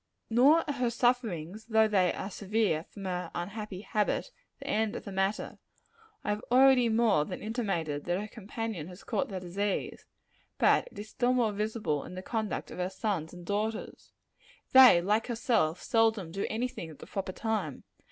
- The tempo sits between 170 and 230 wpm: Yes, average, 180 wpm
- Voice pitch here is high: Yes, high, 210 Hz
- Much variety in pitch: No, average, 3.7 semitones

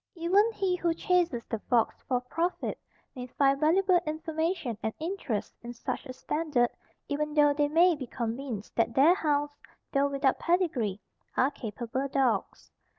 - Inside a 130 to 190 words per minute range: Yes, average, 150 wpm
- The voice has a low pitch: No, very high, 285 Hz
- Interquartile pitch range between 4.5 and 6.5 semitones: Yes, average, 5.1 semitones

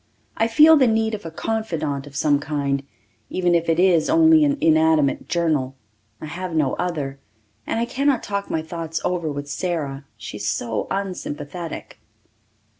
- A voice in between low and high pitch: Yes, medium, 165 Hz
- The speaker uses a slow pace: No, average, 165 wpm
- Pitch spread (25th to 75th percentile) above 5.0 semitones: Yes, wide, 5.6 semitones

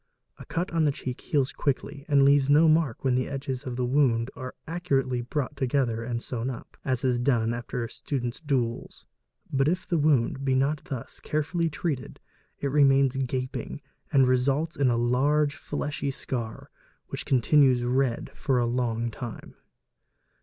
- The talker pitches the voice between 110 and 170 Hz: Yes, low, 135 Hz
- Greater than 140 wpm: Yes, average, 165 wpm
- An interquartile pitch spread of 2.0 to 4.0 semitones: Yes, average, 2.8 semitones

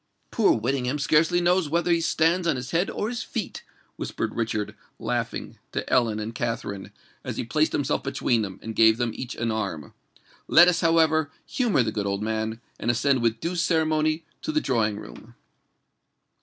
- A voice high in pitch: No, low, 130 Hz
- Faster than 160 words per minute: Yes, average, 180 wpm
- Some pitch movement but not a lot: No, wide, 7.0 semitones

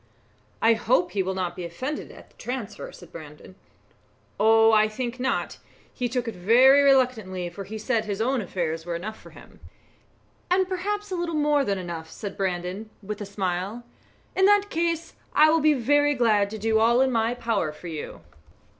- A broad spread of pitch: Yes, wide, 6.0 semitones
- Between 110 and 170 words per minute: No, average, 190 wpm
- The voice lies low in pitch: No, high, 225 Hz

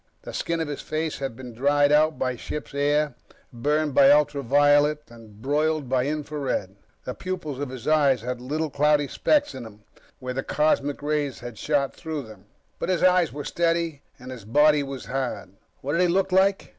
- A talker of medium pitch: Yes, medium, 145 Hz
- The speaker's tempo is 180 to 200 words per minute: Yes, average, 195 wpm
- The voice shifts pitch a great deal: No, average, 2.9 semitones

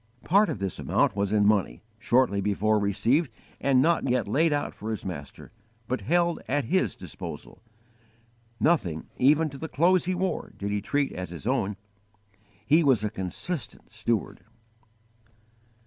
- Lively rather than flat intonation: Yes, wide, 7.4 semitones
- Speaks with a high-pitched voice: No, low, 120 Hz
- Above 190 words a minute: No, average, 155 wpm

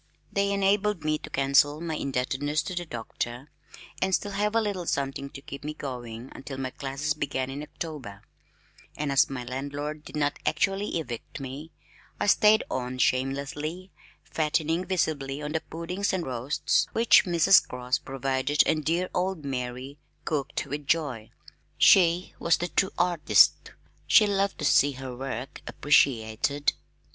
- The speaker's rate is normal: Yes, average, 155 wpm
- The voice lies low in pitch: No, medium, 150 Hz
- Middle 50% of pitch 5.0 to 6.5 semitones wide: No, average, 4.2 semitones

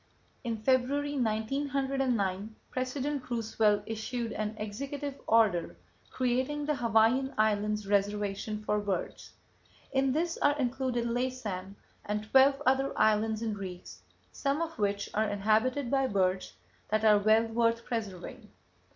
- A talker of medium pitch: No, high, 225 Hz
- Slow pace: Yes, slow, 125 wpm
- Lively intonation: No, average, 4.0 semitones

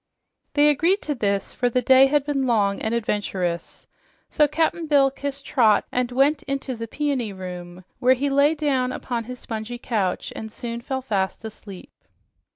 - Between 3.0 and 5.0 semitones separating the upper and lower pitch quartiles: Yes, average, 4.5 semitones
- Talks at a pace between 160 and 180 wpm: Yes, average, 170 wpm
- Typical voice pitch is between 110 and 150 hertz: No, very high, 250 Hz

